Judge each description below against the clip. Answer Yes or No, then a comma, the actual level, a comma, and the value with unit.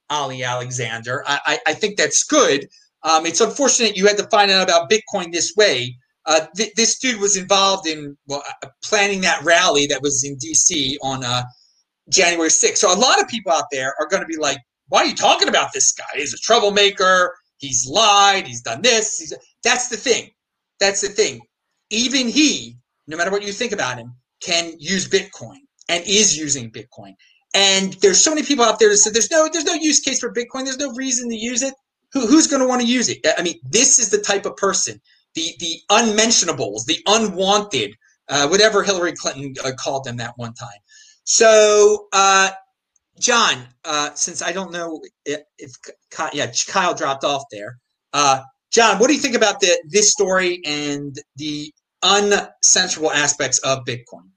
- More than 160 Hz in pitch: Yes, high, 190 Hz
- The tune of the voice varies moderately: No, wide, 7.5 semitones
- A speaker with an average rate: Yes, average, 195 wpm